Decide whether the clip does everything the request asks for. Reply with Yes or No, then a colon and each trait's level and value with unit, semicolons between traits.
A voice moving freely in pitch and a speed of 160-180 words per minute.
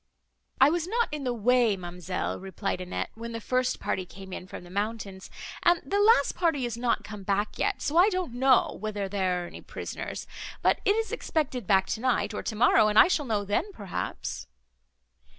No: wide, 6.8 semitones; average, 195 wpm